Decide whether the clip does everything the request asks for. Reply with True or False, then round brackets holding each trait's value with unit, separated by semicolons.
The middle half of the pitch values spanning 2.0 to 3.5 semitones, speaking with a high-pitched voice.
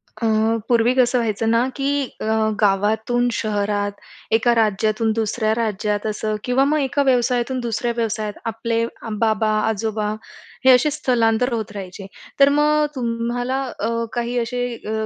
True (2.4 semitones; 230 Hz)